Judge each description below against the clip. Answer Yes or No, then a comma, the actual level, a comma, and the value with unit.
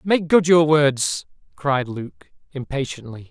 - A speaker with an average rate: No, slow, 125 wpm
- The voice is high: No, medium, 140 Hz